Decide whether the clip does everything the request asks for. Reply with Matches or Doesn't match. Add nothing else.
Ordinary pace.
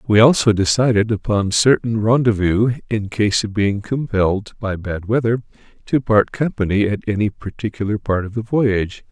Matches